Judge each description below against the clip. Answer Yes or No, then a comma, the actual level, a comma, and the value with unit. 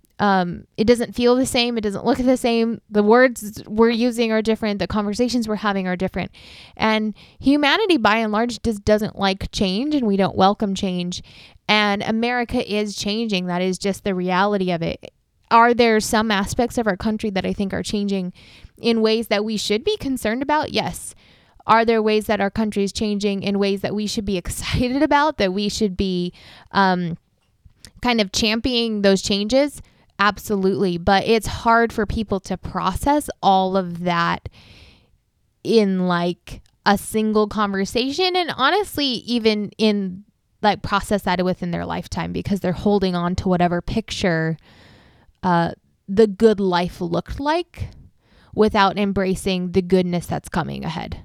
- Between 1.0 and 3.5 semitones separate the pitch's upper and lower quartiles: Yes, average, 3.2 semitones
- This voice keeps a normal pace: Yes, average, 165 wpm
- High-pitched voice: Yes, high, 205 Hz